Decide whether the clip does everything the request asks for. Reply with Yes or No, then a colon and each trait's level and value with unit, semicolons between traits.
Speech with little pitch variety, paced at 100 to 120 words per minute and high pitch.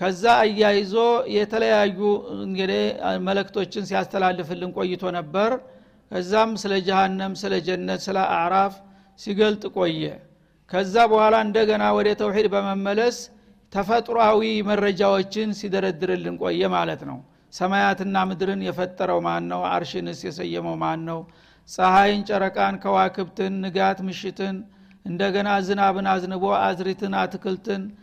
Yes: narrow, 2.0 semitones; average, 105 wpm; high, 195 Hz